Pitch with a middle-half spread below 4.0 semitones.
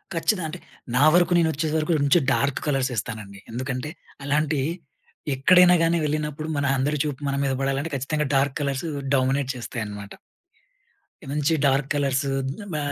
Yes: narrow, 2.6 semitones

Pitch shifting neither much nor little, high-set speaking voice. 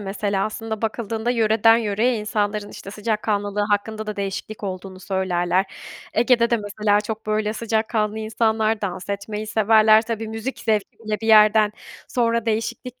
No: narrow, 1.4 semitones; high, 215 Hz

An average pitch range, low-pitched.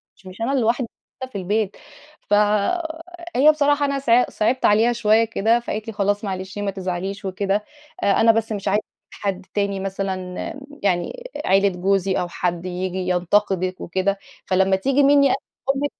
No: average, 4.0 semitones; high, 205 Hz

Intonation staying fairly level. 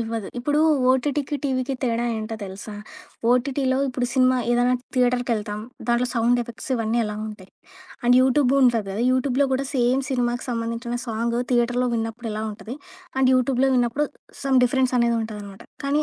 Yes: narrow, 2.2 semitones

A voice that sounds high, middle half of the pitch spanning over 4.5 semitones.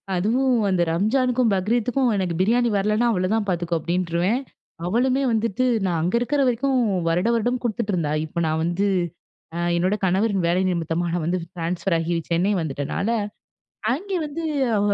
Yes: high, 195 Hz; wide, 5.6 semitones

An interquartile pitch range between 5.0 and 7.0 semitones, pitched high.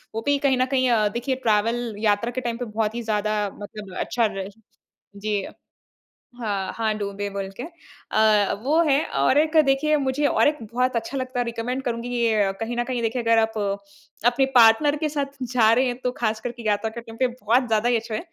No: average, 3.0 semitones; high, 235 Hz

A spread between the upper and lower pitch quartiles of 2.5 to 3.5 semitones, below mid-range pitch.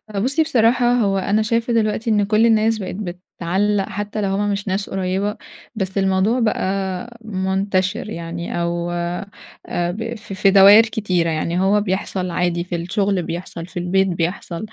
No: average, 2.9 semitones; high, 195 Hz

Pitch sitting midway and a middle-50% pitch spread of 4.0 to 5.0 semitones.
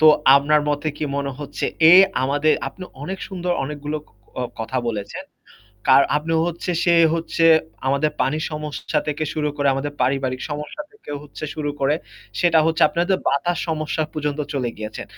No: medium, 150 Hz; narrow, 2.5 semitones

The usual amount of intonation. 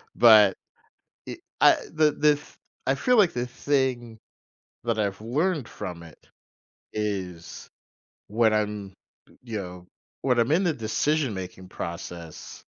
No: wide, 6.1 semitones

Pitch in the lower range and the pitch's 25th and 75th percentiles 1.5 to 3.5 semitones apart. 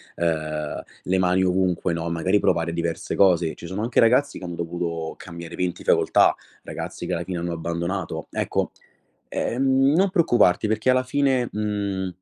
No: very low, 90 Hz; average, 4.4 semitones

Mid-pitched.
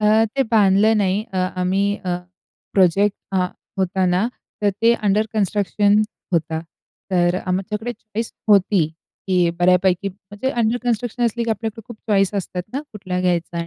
No: high, 200 Hz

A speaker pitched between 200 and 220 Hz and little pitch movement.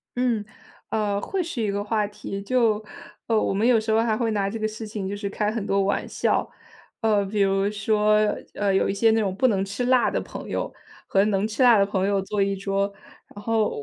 Yes: high, 210 Hz; narrow, 2.0 semitones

